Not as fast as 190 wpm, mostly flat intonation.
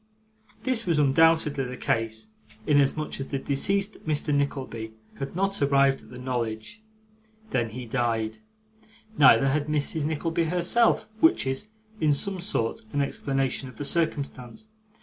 No: average, 140 wpm; average, 4.3 semitones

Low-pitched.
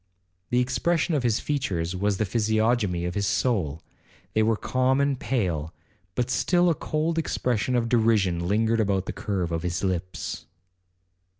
Yes: low, 110 Hz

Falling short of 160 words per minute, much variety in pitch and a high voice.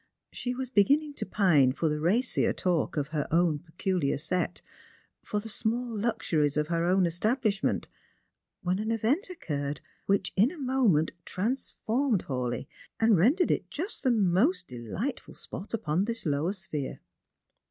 Yes: average, 150 wpm; wide, 7.0 semitones; high, 195 Hz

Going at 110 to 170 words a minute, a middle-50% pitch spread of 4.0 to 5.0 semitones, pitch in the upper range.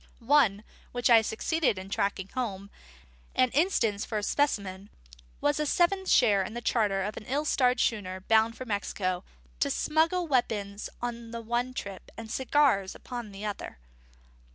Yes: average, 165 wpm; average, 4.4 semitones; high, 225 Hz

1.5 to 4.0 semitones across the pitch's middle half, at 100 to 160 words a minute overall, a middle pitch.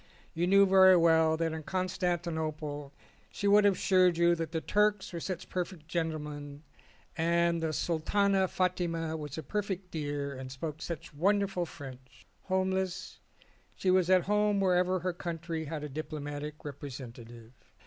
Yes: average, 3.6 semitones; average, 150 wpm; medium, 170 Hz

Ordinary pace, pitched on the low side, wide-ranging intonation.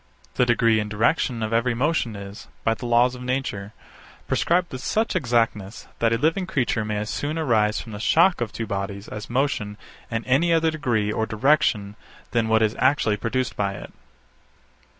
No: average, 185 wpm; low, 115 Hz; average, 3.8 semitones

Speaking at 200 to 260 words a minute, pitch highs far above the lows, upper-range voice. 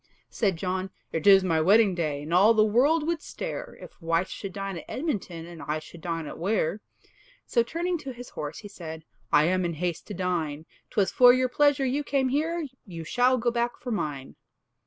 Yes: fast, 205 wpm; wide, 7.0 semitones; high, 195 Hz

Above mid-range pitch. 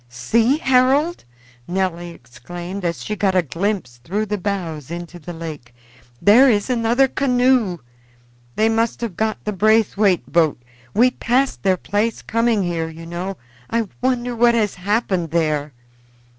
Yes: high, 200 Hz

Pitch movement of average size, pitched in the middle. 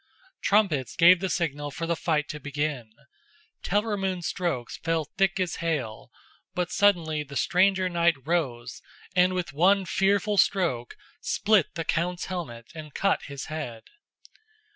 Yes: average, 4.1 semitones; medium, 170 Hz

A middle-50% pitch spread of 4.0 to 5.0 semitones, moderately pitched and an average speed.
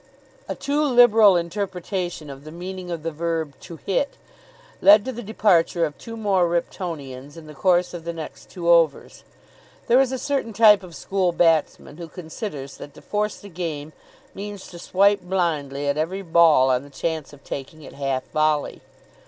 Yes: average, 4.5 semitones; medium, 170 Hz; average, 180 wpm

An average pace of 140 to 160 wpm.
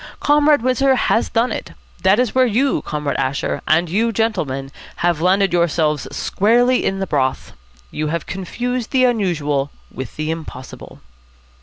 Yes: average, 150 wpm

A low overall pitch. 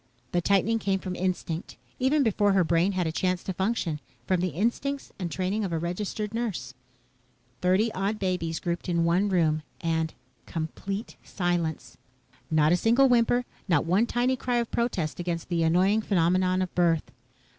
No: medium, 185 Hz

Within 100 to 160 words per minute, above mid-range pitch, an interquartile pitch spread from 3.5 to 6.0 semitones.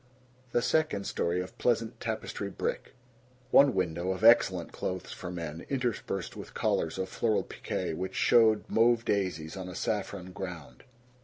No: average, 150 wpm; very low, 95 Hz; average, 4.1 semitones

